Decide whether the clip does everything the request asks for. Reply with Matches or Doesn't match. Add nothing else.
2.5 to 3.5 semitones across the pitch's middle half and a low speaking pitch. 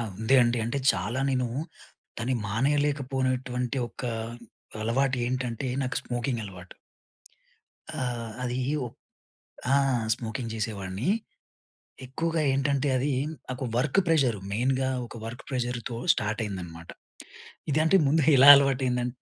Matches